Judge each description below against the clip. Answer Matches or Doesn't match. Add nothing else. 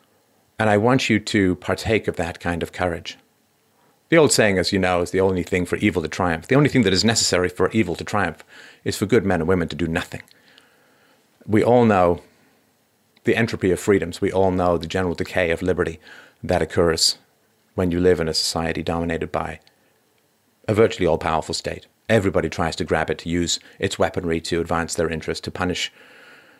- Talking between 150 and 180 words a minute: Doesn't match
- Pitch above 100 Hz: Doesn't match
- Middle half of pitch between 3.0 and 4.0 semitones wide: Matches